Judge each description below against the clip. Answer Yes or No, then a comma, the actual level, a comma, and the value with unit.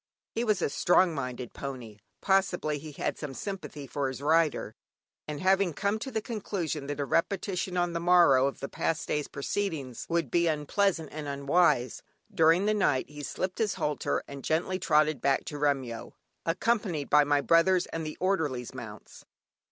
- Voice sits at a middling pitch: Yes, medium, 155 Hz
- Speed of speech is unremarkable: Yes, average, 175 wpm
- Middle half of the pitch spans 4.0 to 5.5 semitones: Yes, average, 4.7 semitones